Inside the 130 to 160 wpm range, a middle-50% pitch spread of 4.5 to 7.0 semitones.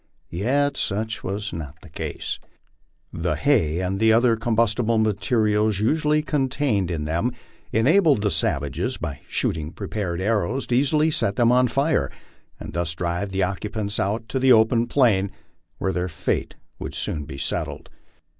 Yes: average, 150 wpm; wide, 5.6 semitones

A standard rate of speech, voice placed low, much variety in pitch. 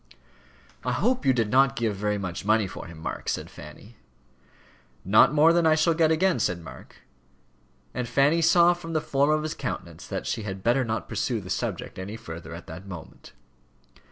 Yes: average, 190 wpm; low, 120 Hz; wide, 8.2 semitones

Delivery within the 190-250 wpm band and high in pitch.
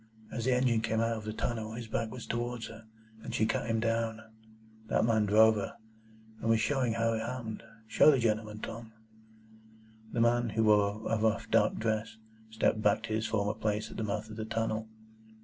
No: average, 200 wpm; low, 110 Hz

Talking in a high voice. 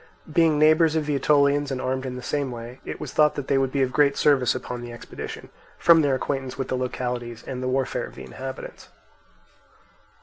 No: low, 135 Hz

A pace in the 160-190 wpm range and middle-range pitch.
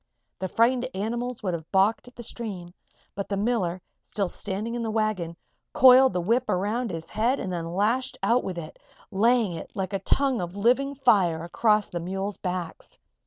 No: average, 185 wpm; high, 205 Hz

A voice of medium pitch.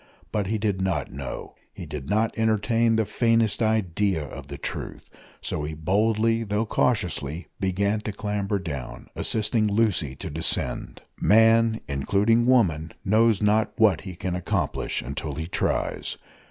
No: low, 105 Hz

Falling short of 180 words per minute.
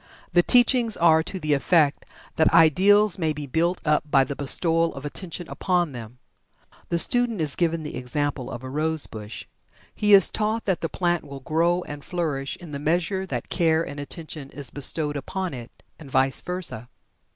No: average, 185 wpm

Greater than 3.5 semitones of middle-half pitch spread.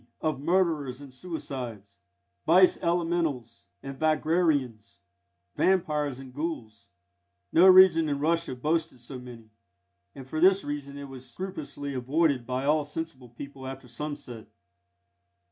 Yes: average, 4.3 semitones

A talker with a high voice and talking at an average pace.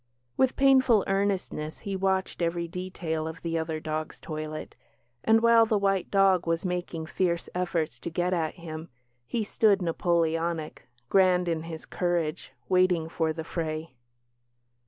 No: medium, 170 Hz; average, 145 wpm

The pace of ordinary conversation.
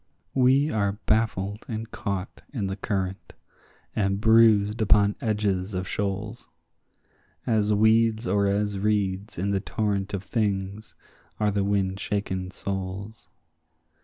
No: slow, 125 wpm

